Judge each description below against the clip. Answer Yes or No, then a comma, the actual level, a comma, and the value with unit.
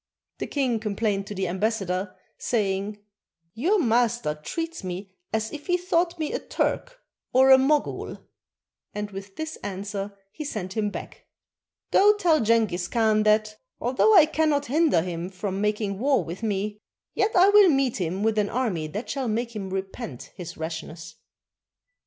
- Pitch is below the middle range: No, high, 215 Hz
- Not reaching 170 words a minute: Yes, average, 160 wpm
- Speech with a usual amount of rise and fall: No, wide, 6.2 semitones